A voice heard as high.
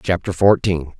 No: very low, 90 Hz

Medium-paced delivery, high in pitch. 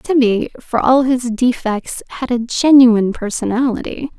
No: slow, 130 wpm; high, 245 Hz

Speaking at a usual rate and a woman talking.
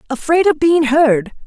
Yes: average, 165 wpm; female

